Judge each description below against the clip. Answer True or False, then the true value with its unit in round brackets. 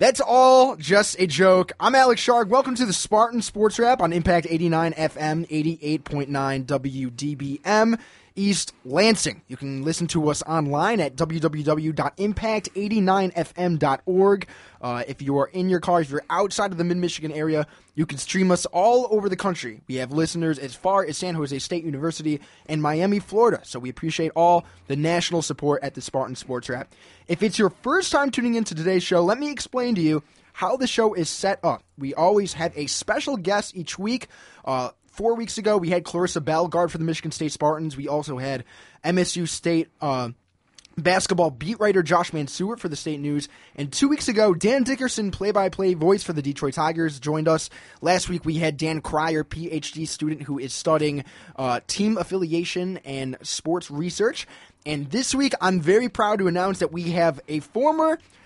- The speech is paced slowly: False (185 wpm)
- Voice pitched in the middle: True (170 Hz)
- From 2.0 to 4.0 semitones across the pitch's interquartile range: False (4.7 semitones)